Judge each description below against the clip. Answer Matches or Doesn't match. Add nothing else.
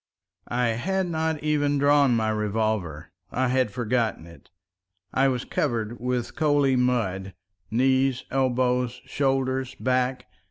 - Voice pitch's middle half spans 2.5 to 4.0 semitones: Matches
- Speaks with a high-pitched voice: Doesn't match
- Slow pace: Matches